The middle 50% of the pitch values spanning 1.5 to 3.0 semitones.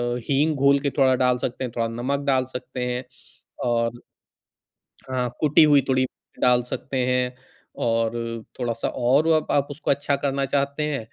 Yes: narrow, 2.4 semitones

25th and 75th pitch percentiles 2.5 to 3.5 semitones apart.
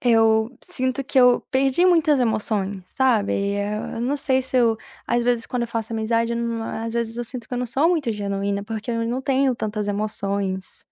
Yes: average, 2.9 semitones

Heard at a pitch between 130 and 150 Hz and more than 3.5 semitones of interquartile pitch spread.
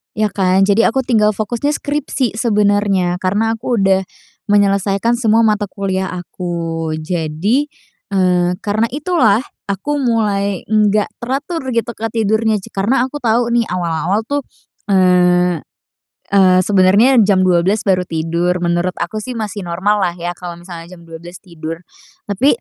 No: high, 200 Hz; average, 3.9 semitones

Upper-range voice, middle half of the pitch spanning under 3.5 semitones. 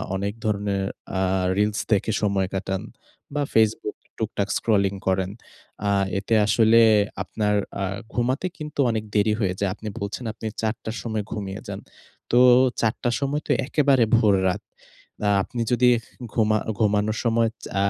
No: low, 110 Hz; narrow, 2.5 semitones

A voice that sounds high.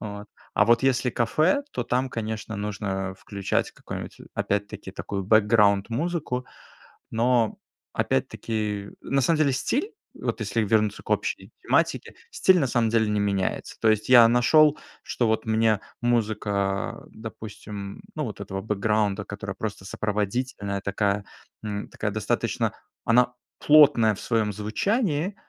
No: low, 110 Hz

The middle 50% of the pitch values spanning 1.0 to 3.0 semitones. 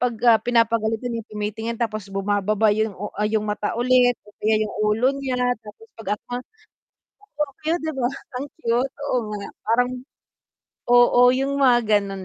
Yes: average, 2.7 semitones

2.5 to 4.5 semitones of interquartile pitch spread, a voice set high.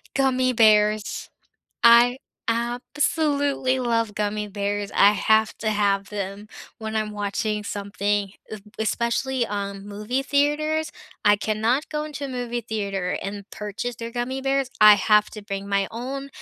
Yes: average, 3.7 semitones; high, 220 Hz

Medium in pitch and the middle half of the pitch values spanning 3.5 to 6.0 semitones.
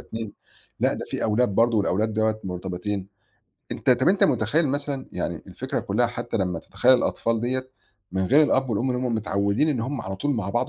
No: low, 115 Hz; average, 4.4 semitones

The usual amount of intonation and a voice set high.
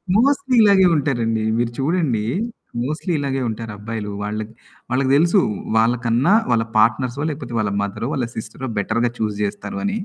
No: average, 5.0 semitones; low, 120 Hz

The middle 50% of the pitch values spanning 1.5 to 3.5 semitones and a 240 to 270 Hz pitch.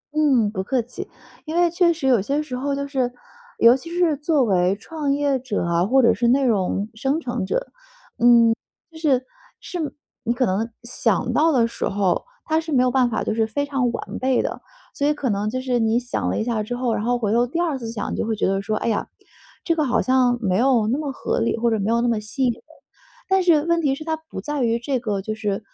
No: average, 4.4 semitones; very high, 250 Hz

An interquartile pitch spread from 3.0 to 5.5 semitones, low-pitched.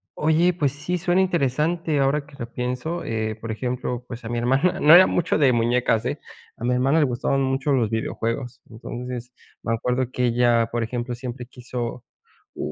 Yes: average, 3.5 semitones; low, 125 Hz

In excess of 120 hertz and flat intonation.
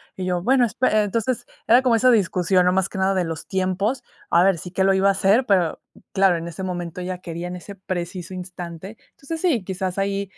Yes: high, 190 Hz; narrow, 2.2 semitones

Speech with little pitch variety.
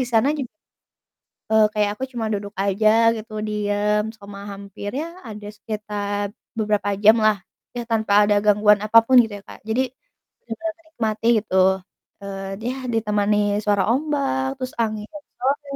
Yes: narrow, 1.8 semitones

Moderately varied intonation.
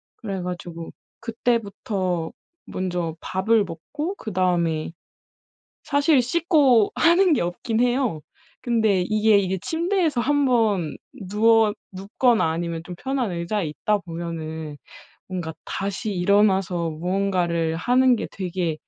No: wide, 5.7 semitones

